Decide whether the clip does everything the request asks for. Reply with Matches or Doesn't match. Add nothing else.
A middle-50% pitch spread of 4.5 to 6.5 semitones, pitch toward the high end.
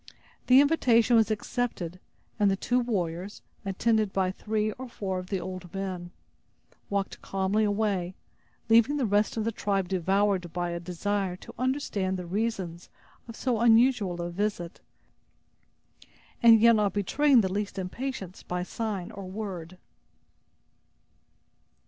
Doesn't match